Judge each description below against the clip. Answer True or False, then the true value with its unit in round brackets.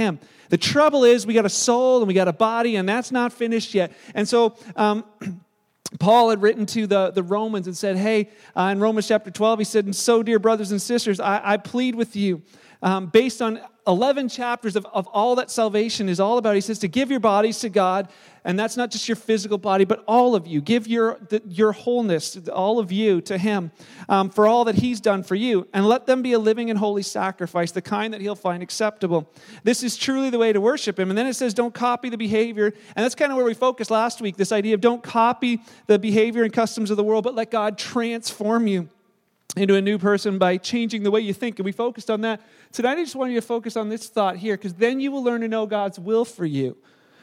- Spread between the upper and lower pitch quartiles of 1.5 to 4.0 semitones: True (2.7 semitones)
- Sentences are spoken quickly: True (245 wpm)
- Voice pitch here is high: True (215 Hz)